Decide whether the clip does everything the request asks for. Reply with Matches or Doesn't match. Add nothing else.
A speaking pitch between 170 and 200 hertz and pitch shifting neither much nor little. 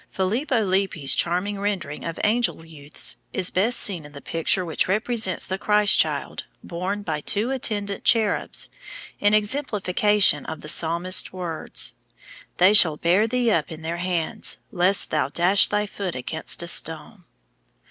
Matches